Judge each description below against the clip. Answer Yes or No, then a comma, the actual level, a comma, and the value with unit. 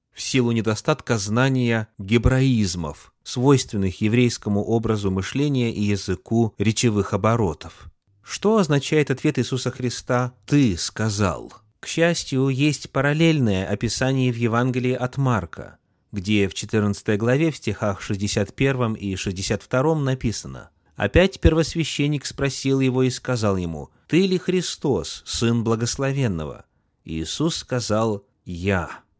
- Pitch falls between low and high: No, low, 120 Hz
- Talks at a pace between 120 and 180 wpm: No, slow, 110 wpm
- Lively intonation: No, average, 4.7 semitones